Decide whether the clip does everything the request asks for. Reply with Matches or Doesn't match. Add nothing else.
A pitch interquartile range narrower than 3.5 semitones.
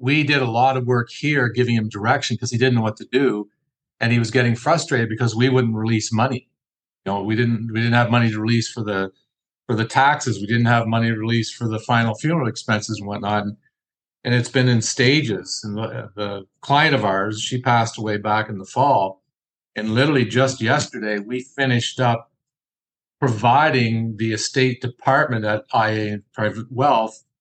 Matches